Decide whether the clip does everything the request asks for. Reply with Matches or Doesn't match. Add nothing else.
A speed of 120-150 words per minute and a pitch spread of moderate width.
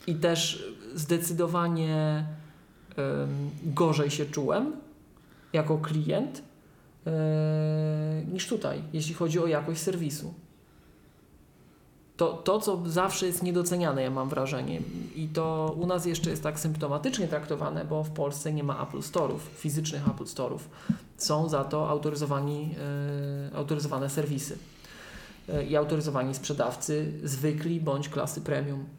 Doesn't match